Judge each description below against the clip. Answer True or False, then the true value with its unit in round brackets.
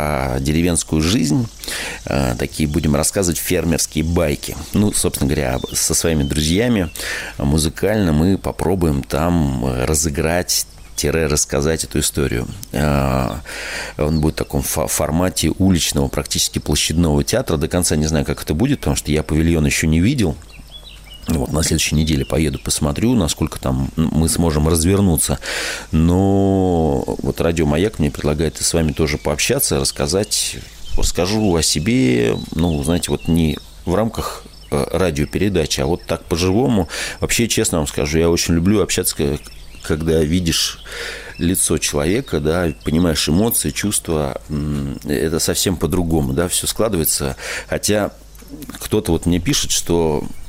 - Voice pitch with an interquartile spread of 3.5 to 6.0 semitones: False (2.6 semitones)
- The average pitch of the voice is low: True (80 Hz)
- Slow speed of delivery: False (130 wpm)